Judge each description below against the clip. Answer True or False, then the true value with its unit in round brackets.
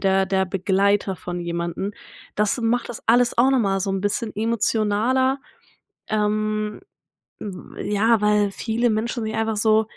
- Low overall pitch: False (210 Hz)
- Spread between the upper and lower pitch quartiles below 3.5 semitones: True (2.5 semitones)